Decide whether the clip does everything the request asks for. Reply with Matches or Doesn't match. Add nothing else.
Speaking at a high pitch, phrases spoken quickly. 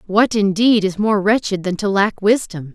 Doesn't match